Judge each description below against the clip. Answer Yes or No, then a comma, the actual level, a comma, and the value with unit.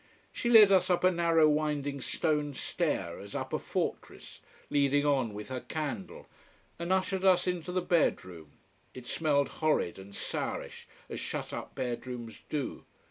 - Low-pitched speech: No, medium, 145 Hz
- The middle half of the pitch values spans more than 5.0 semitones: Yes, wide, 5.4 semitones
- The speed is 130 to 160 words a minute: Yes, average, 150 wpm